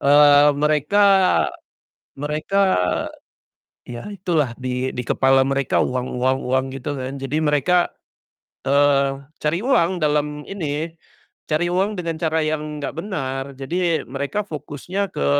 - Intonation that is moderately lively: Yes, average, 3.7 semitones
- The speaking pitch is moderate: Yes, medium, 150 Hz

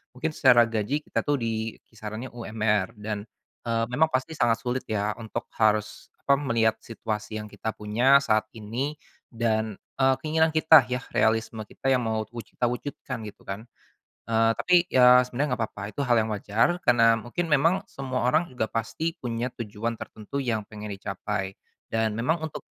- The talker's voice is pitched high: No, low, 115 Hz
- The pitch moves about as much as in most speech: Yes, average, 3.2 semitones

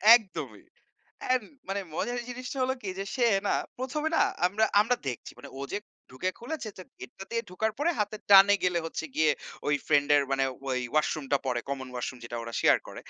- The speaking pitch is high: Yes, high, 195 Hz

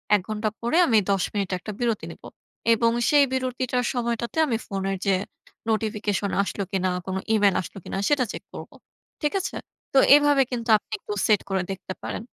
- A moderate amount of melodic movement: Yes, average, 4.0 semitones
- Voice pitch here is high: Yes, high, 220 Hz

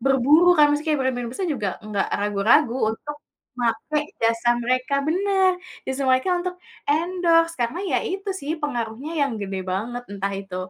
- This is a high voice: Yes, very high, 270 Hz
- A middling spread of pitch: No, wide, 6.0 semitones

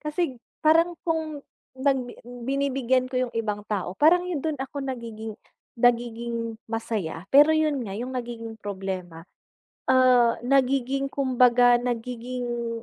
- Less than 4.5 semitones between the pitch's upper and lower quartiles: Yes, average, 3.1 semitones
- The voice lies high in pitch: Yes, high, 245 Hz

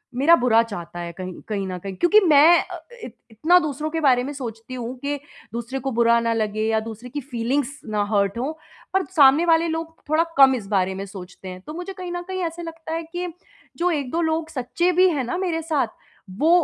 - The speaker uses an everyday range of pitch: No, wide, 6.5 semitones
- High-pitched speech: Yes, very high, 275 Hz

